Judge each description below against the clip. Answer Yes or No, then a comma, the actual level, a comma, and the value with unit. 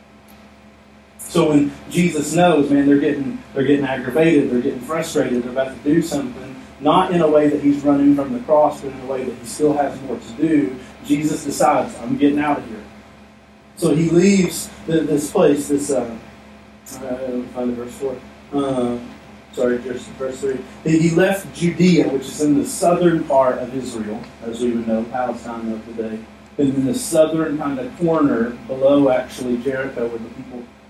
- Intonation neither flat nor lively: Yes, average, 3.6 semitones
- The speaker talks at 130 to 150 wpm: No, average, 190 wpm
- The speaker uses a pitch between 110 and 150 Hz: Yes, medium, 140 Hz